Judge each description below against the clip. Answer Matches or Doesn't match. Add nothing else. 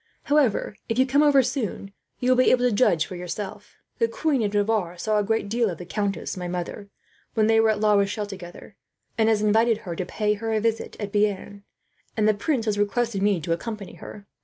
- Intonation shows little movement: Matches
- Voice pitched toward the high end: Matches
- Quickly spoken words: Matches